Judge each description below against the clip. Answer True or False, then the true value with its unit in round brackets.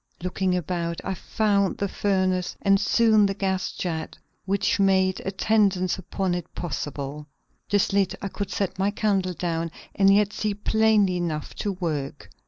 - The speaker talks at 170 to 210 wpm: False (155 wpm)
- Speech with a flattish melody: True (2.2 semitones)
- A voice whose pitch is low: False (190 Hz)